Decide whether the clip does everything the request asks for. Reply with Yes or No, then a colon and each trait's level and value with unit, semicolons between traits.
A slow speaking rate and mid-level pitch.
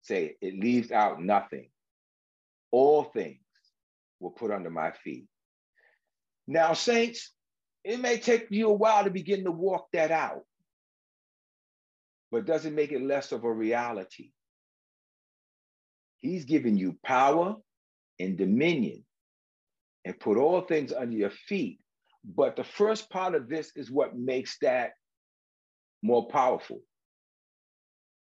Yes: slow, 125 wpm; medium, 155 Hz